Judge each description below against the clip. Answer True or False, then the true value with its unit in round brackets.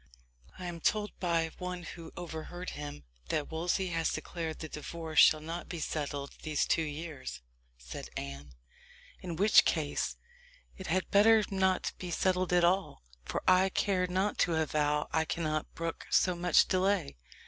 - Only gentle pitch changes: False (3.0 semitones)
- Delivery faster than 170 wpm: False (160 wpm)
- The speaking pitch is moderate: True (170 Hz)